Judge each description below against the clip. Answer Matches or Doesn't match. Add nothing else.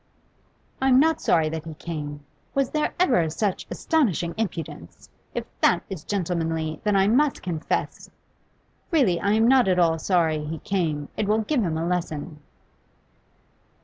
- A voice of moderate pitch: Matches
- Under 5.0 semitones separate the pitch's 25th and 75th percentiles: Doesn't match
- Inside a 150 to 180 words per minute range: Matches